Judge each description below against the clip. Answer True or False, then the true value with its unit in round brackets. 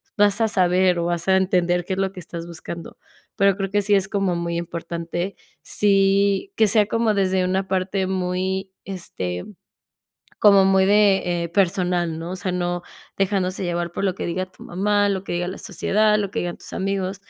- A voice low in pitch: False (190 Hz)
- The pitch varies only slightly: True (2.0 semitones)